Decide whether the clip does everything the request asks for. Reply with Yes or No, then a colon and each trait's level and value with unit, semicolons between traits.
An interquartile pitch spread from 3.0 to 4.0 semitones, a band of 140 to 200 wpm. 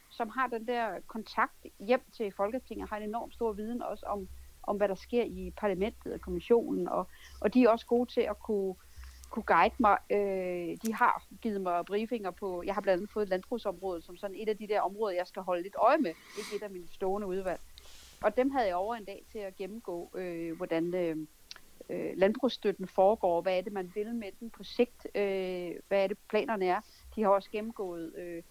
No: average, 3.6 semitones; average, 215 wpm